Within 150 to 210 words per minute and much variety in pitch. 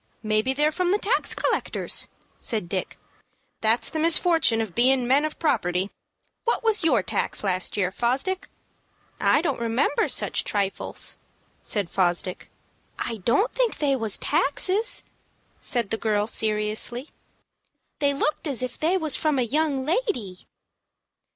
No: average, 140 wpm; wide, 6.6 semitones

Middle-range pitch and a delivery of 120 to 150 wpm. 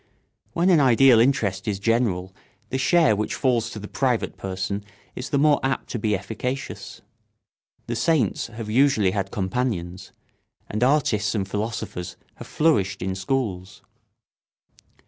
No: low, 115 Hz; average, 140 wpm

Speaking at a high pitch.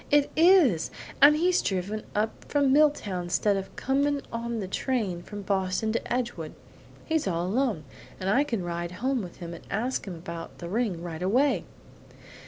Yes: high, 210 Hz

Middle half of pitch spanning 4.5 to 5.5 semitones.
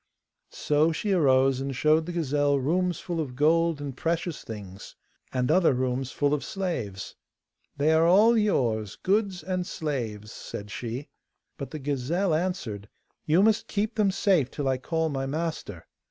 Yes: average, 5.2 semitones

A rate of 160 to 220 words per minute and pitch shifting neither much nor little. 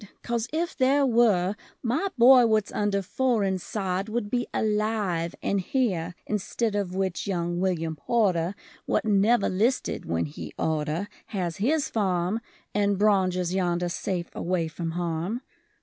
No: average, 140 wpm; average, 4.2 semitones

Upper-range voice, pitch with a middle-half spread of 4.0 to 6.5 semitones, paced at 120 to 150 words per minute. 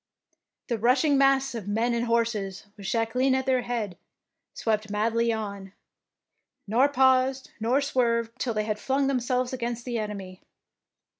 No: high, 235 Hz; average, 3.2 semitones; average, 145 wpm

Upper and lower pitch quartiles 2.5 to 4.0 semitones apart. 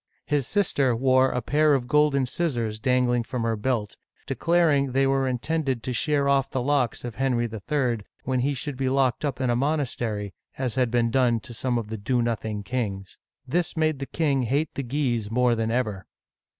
Yes: average, 3.0 semitones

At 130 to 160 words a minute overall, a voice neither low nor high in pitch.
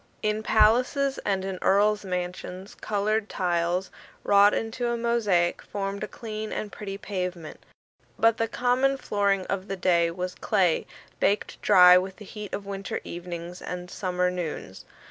No: average, 150 wpm; high, 195 Hz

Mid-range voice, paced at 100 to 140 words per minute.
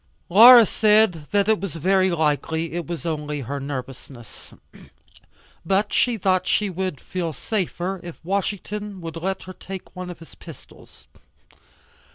Yes: medium, 180 Hz; slow, 135 wpm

